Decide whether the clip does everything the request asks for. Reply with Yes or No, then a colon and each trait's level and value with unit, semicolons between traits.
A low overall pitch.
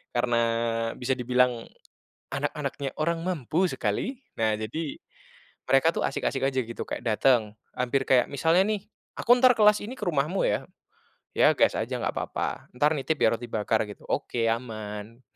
Yes: low, 130 Hz